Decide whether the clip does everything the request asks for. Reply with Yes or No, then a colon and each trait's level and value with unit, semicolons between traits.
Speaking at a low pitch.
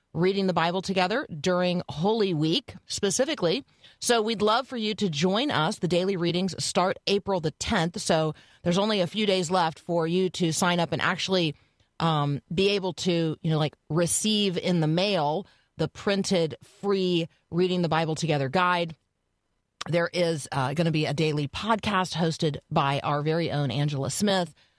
No: medium, 170 Hz